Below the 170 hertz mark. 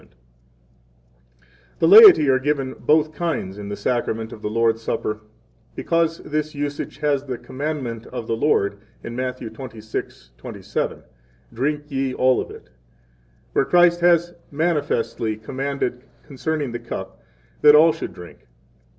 Yes: low, 135 Hz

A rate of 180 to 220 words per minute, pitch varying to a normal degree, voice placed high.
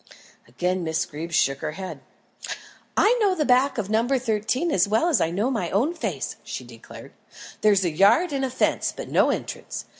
No: average, 190 wpm; wide, 7.2 semitones; high, 215 Hz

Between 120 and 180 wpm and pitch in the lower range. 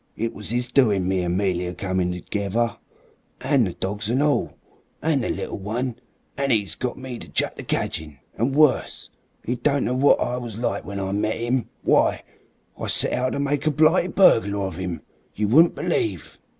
No: average, 190 wpm; low, 115 Hz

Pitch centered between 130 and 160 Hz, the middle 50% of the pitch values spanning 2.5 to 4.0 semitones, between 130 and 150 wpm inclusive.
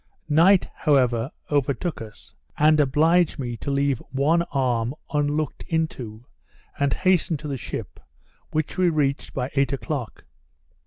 Yes: medium, 140 Hz; average, 3.2 semitones; slow, 135 wpm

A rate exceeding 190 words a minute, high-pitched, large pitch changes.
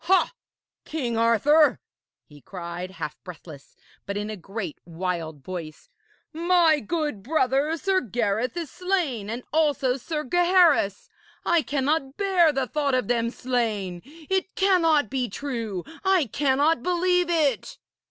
No: slow, 135 wpm; very high, 270 Hz; wide, 7.8 semitones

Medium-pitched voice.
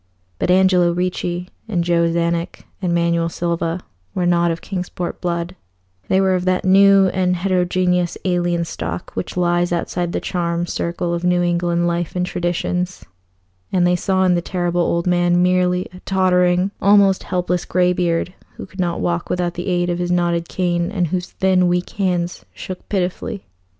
Yes: medium, 180 Hz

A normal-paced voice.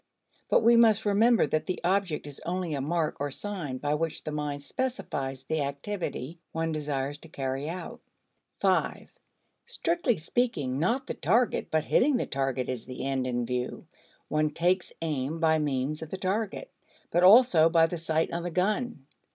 Yes: average, 170 wpm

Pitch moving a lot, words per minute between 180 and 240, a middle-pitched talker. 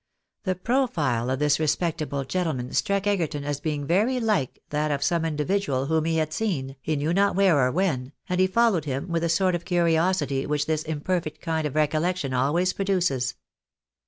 No: average, 4.2 semitones; average, 185 wpm; medium, 160 Hz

